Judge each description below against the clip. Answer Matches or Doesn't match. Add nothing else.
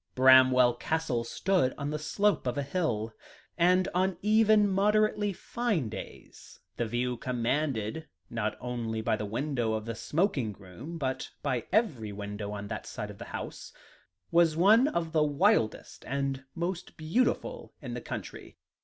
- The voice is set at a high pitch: Doesn't match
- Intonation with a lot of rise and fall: Matches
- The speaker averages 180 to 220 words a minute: Doesn't match